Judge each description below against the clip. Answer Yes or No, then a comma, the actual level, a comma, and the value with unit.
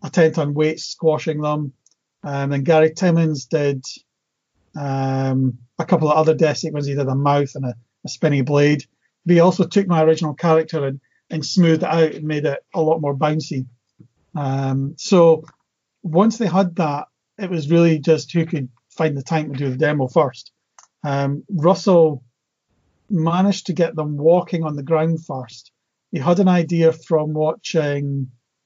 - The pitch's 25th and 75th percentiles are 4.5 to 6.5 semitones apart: No, average, 3.0 semitones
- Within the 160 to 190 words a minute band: Yes, average, 175 wpm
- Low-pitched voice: No, medium, 155 Hz